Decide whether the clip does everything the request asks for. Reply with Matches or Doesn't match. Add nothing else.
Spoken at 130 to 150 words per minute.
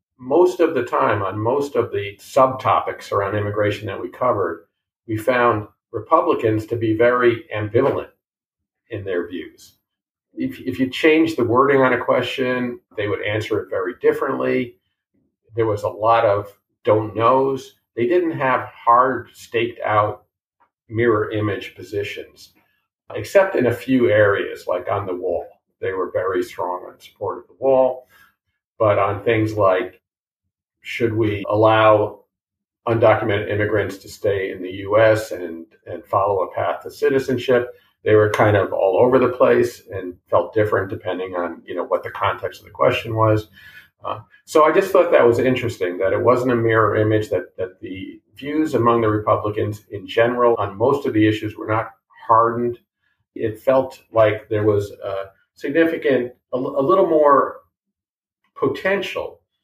Doesn't match